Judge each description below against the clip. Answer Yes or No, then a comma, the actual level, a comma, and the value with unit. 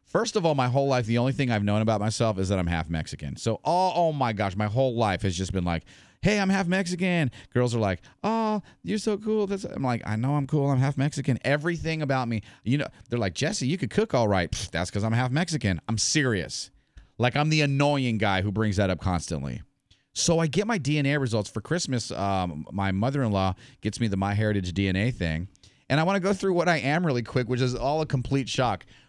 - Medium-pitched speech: No, low, 125 Hz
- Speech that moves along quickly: Yes, fast, 245 wpm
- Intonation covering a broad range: Yes, wide, 6.6 semitones